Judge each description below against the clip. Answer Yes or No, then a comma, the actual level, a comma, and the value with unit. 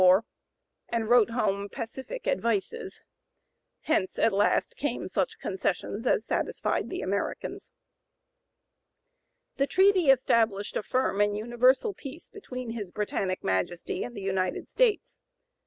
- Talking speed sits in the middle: No, slow, 125 wpm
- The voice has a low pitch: No, high, 230 Hz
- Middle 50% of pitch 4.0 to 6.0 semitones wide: Yes, average, 5.2 semitones